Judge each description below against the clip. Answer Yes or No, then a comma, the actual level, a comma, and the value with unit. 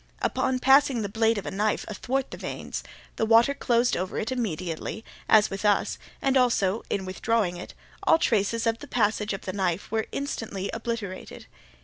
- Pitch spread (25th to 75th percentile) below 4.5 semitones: Yes, average, 3.4 semitones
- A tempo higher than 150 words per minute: Yes, average, 175 wpm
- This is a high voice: Yes, high, 220 Hz